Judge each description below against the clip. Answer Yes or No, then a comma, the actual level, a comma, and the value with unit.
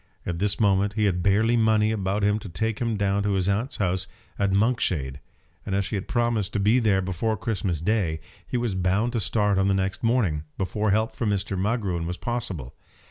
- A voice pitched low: Yes, low, 100 Hz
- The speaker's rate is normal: No, fast, 210 wpm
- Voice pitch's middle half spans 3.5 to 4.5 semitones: No, average, 2.7 semitones